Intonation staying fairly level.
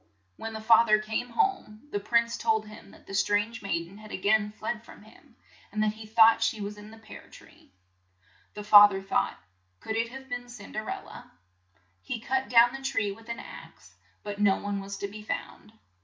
Yes: narrow, 2.1 semitones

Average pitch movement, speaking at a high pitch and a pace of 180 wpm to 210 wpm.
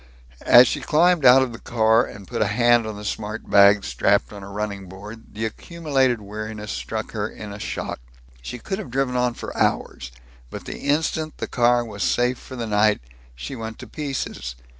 No: average, 3.3 semitones; low, 115 Hz; average, 200 wpm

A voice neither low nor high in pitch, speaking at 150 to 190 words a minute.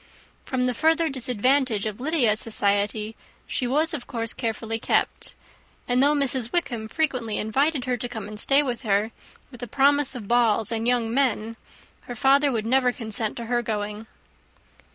No: high, 240 Hz; average, 170 wpm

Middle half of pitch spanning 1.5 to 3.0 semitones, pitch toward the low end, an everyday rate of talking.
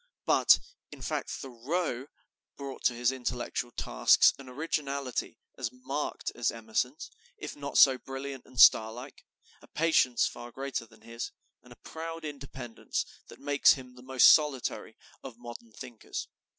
Yes: average, 2.7 semitones; low, 130 Hz; average, 150 wpm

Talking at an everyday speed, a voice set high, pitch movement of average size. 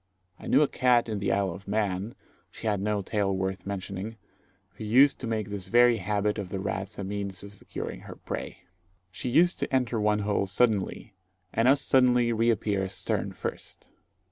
No: average, 185 wpm; low, 105 Hz; average, 3.0 semitones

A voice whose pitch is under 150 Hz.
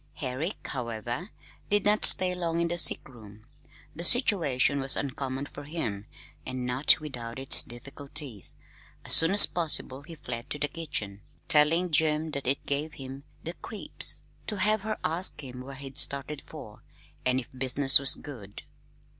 Yes: medium, 140 Hz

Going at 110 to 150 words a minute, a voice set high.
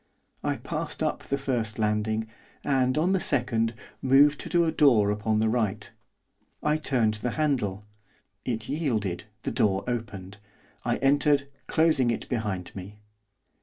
No: average, 140 wpm; low, 115 Hz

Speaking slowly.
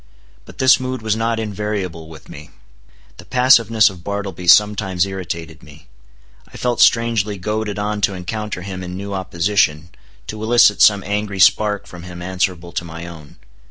No: average, 160 wpm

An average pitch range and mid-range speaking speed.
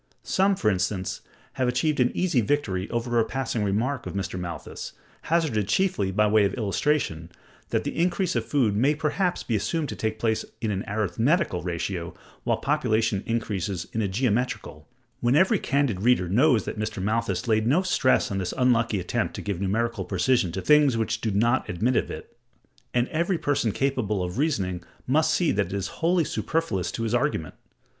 No: wide, 6.2 semitones; average, 185 wpm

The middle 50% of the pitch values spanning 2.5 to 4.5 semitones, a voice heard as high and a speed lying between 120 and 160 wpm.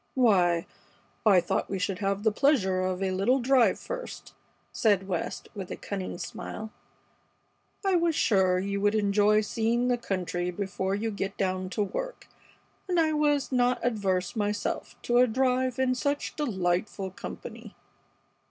No: average, 4.9 semitones; high, 210 Hz; average, 150 wpm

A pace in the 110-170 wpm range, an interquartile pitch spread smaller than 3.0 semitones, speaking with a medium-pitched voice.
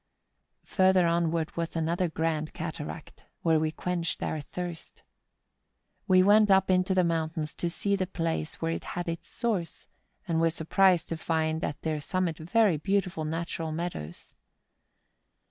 Yes: average, 150 wpm; narrow, 2.4 semitones; medium, 165 Hz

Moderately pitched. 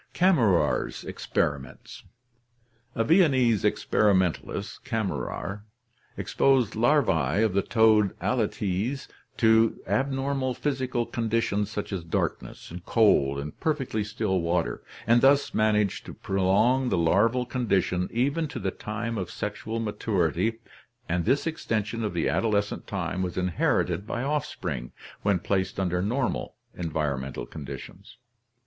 No: low, 105 Hz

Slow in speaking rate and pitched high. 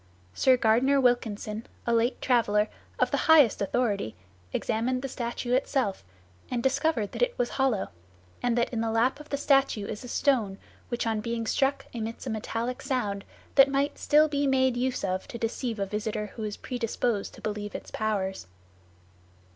No: average, 175 wpm; high, 235 Hz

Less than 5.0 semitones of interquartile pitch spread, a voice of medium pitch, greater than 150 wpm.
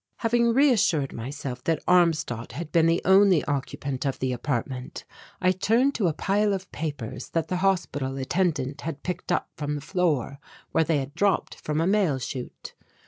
No: wide, 5.4 semitones; medium, 160 Hz; average, 175 wpm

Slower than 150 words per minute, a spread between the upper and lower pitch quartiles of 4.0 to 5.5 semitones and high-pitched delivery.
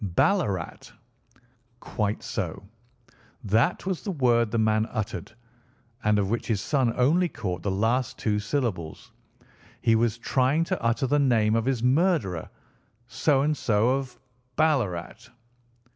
No: slow, 135 wpm; average, 4.4 semitones; low, 120 Hz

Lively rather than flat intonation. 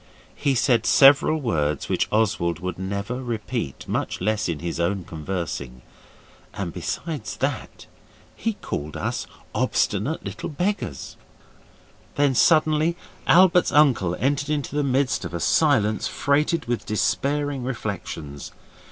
Yes: wide, 8.2 semitones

